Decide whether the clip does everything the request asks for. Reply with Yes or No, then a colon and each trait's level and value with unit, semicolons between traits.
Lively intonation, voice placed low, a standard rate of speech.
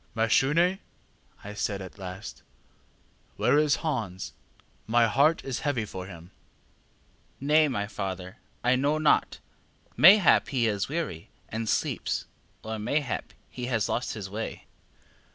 No: wide, 6.3 semitones; low, 115 Hz; slow, 130 wpm